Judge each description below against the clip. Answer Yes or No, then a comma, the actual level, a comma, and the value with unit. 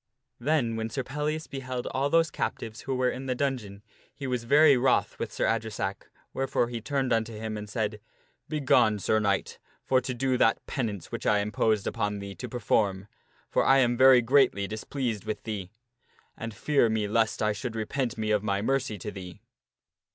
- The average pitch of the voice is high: No, low, 115 Hz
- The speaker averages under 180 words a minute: No, average, 195 wpm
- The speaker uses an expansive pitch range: No, average, 3.8 semitones